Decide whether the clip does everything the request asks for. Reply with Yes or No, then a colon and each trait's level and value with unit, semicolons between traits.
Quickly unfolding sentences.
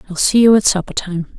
Yes: fast, 260 wpm